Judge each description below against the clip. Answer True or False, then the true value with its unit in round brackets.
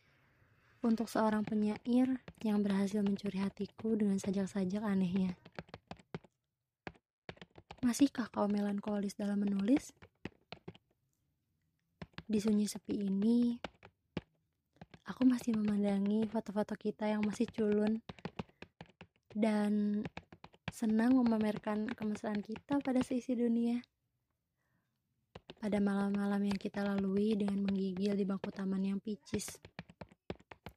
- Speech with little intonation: True (1.9 semitones)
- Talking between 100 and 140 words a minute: False (90 wpm)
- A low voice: False (210 Hz)